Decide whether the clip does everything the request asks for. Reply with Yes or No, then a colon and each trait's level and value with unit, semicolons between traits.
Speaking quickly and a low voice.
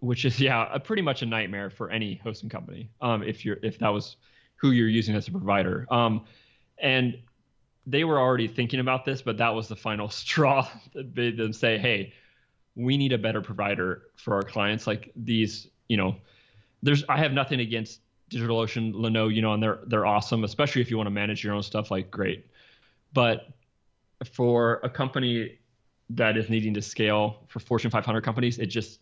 No: average, 195 wpm; low, 115 Hz